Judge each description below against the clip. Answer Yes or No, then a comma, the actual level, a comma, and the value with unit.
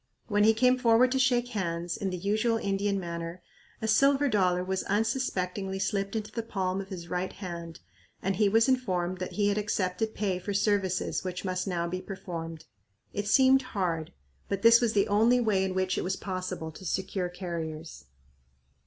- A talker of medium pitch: No, high, 195 Hz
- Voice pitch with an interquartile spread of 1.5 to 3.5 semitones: Yes, average, 3.2 semitones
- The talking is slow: No, average, 190 wpm